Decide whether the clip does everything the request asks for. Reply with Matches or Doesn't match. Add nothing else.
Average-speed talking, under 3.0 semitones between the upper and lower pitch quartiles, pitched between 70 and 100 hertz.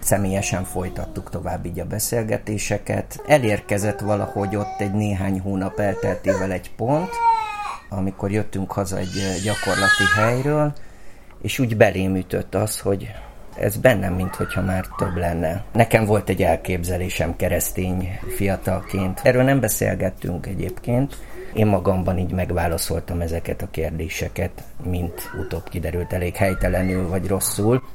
Matches